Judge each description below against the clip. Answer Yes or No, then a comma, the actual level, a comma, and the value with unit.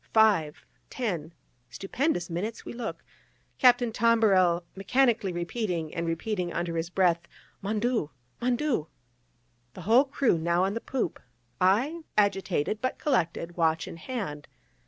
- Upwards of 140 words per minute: No, slow, 135 wpm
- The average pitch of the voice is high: Yes, high, 195 Hz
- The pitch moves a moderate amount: No, wide, 5.7 semitones